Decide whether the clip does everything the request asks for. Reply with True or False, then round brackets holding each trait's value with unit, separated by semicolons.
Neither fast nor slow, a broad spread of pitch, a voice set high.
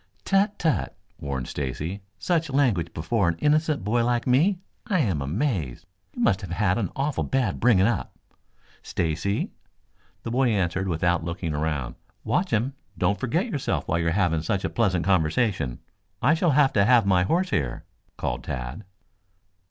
False (165 wpm; 8.2 semitones; 100 Hz)